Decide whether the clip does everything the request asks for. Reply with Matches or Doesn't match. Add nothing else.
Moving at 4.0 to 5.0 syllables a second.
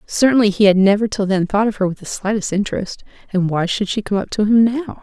Doesn't match